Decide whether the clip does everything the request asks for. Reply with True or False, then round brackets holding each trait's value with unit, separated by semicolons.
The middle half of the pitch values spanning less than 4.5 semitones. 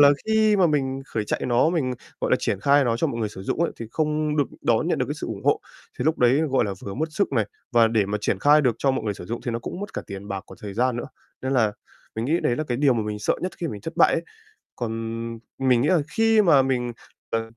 False (5.2 semitones)